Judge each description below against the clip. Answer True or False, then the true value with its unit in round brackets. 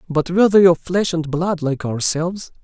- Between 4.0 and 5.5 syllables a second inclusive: True (5.1 syllables/s)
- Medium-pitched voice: True (170 Hz)